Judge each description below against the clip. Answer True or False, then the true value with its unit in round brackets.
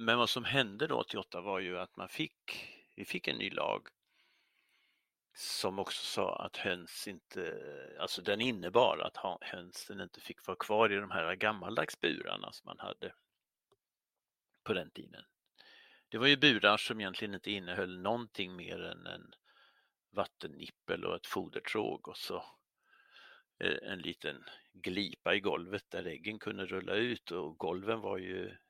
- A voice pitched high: False (120 Hz)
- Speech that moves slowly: False (155 wpm)